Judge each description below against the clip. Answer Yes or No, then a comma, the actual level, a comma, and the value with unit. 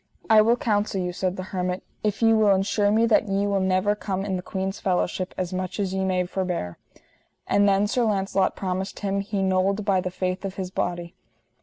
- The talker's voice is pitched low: No, high, 190 Hz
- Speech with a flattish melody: Yes, narrow, 1.6 semitones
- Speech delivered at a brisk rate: Yes, fast, 210 wpm